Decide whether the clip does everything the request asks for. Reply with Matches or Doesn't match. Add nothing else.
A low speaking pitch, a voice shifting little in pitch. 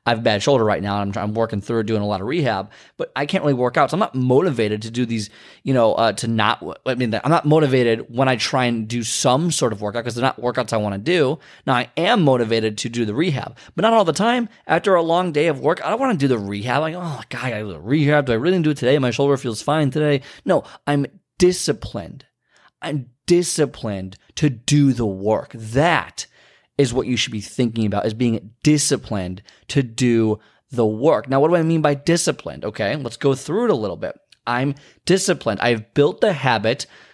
Doesn't match